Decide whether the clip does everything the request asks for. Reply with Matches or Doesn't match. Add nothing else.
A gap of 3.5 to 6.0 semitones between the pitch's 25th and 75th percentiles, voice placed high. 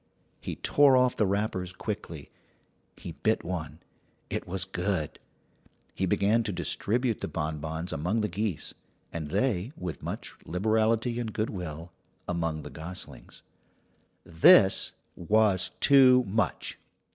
Doesn't match